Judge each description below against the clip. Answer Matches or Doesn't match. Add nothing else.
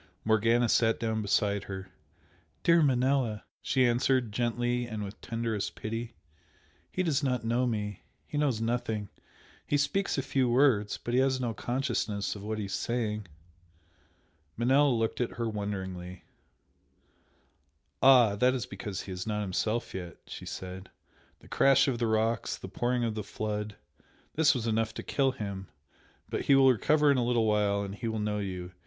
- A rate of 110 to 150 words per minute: Doesn't match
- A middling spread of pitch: Matches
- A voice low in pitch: Matches